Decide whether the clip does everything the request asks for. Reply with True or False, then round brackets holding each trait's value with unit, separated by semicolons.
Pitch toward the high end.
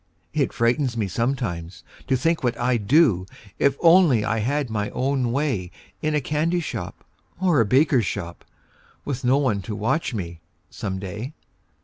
False (125 Hz)